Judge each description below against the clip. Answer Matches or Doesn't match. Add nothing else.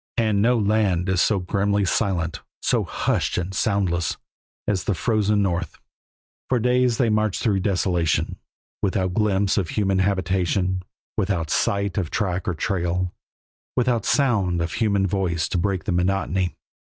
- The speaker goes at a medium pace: Matches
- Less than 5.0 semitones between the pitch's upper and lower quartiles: Matches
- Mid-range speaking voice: Doesn't match